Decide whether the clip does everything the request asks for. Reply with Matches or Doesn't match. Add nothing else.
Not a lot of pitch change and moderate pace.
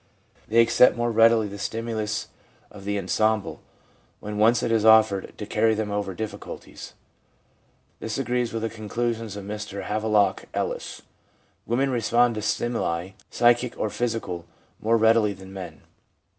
Matches